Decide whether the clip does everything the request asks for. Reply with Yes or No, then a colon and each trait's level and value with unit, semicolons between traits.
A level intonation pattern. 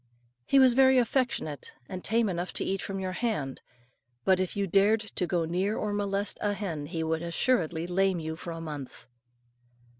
No: average, 4.1 semitones